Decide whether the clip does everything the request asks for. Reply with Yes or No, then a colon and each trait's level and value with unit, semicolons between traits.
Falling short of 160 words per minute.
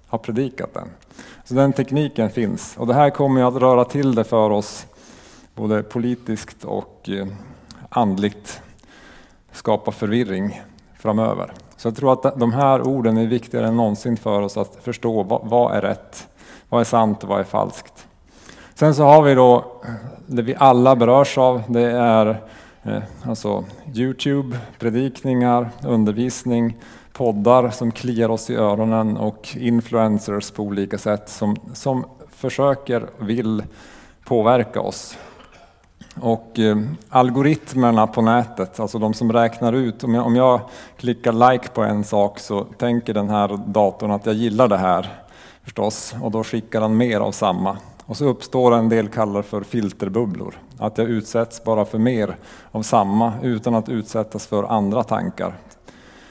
Yes: average, 150 wpm